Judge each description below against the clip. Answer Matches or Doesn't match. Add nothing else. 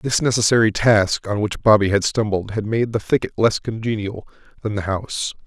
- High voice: Doesn't match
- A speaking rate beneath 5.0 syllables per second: Doesn't match